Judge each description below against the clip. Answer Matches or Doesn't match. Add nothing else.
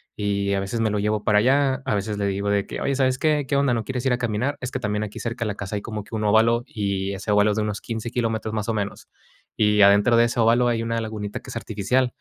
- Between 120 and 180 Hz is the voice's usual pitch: Doesn't match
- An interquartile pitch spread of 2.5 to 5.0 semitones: Matches